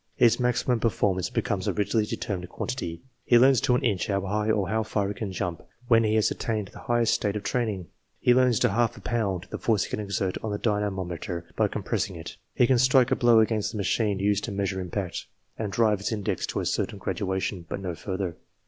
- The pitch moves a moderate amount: Yes, average, 3.1 semitones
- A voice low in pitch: Yes, low, 105 Hz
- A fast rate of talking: Yes, fast, 230 wpm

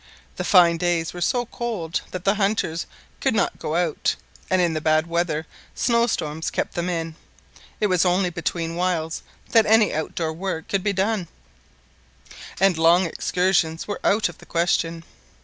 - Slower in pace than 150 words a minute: No, average, 165 wpm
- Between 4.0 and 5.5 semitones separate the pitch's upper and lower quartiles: No, average, 3.0 semitones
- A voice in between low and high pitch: Yes, medium, 175 Hz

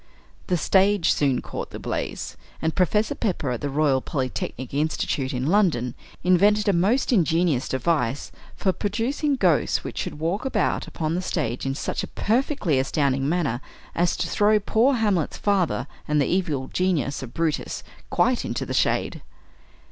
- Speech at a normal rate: Yes, average, 160 wpm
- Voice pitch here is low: No, medium, 165 Hz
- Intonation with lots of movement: Yes, wide, 6.5 semitones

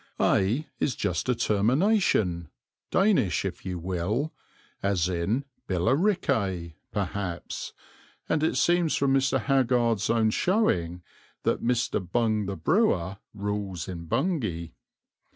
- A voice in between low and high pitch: No, low, 105 Hz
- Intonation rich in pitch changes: Yes, wide, 7.0 semitones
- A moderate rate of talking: No, slow, 115 wpm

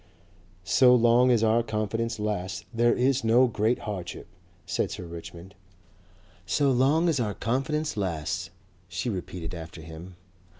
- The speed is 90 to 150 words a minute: Yes, slow, 135 wpm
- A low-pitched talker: Yes, low, 110 Hz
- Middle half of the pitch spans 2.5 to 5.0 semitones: No, wide, 5.4 semitones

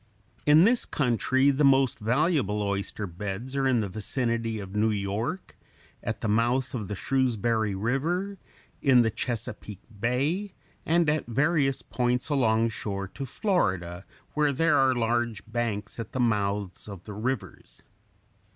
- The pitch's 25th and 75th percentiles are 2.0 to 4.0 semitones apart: No, average, 4.6 semitones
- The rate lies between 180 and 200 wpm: No, average, 140 wpm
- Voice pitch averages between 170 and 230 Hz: No, low, 120 Hz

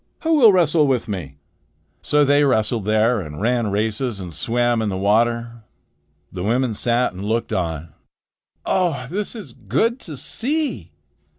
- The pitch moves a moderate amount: No, wide, 5.8 semitones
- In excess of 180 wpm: No, average, 155 wpm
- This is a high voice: No, low, 120 Hz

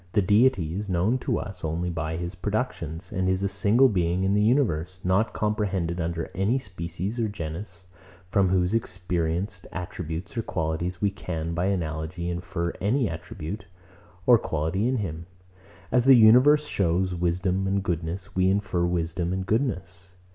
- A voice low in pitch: Yes, very low, 90 Hz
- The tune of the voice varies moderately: Yes, average, 3.3 semitones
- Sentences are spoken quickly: No, average, 160 wpm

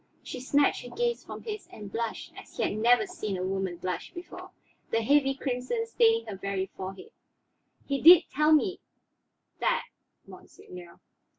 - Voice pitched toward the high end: Yes, very high, 270 Hz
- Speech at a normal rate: Yes, average, 160 wpm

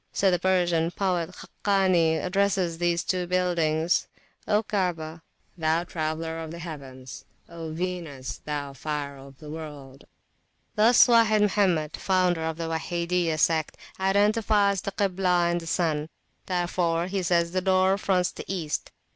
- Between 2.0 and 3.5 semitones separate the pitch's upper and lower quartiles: Yes, average, 2.7 semitones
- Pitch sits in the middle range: Yes, medium, 175 Hz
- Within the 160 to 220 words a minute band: No, average, 140 wpm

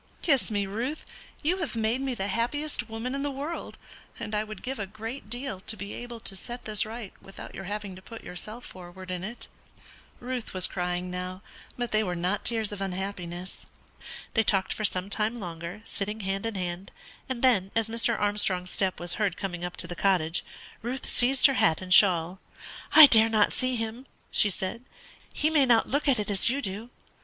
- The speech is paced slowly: No, fast, 205 wpm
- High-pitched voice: Yes, high, 210 Hz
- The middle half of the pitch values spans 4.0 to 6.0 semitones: Yes, average, 4.4 semitones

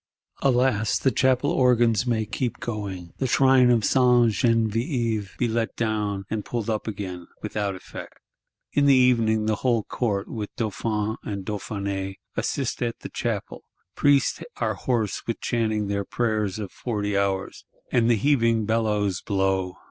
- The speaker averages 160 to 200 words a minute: No, average, 150 wpm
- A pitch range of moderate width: Yes, average, 3.1 semitones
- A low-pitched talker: Yes, low, 110 Hz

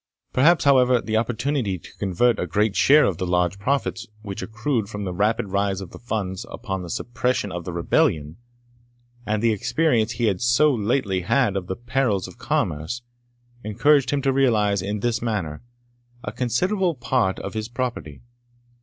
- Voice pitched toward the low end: Yes, low, 110 Hz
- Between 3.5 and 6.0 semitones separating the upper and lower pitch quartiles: Yes, average, 4.6 semitones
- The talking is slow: No, average, 170 wpm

